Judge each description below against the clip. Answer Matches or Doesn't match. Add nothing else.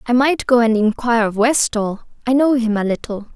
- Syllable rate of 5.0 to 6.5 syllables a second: Matches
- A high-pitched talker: Matches